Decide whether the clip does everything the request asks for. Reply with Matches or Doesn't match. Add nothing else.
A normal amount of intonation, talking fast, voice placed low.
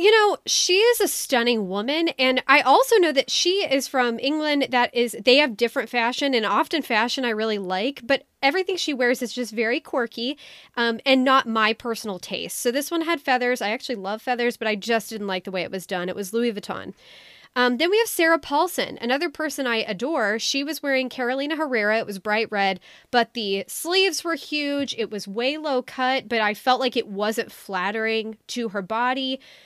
Doesn't match